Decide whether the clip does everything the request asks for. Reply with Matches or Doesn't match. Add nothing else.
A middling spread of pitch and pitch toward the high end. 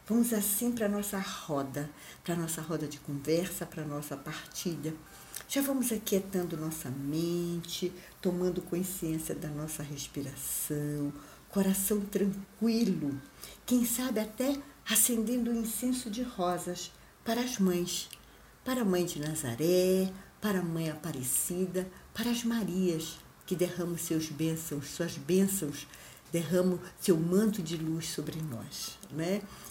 Doesn't match